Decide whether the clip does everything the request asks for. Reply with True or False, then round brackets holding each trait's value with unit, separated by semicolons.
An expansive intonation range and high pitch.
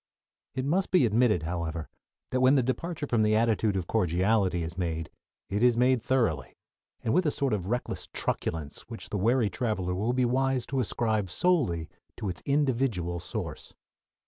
False (6.2 semitones; 110 Hz)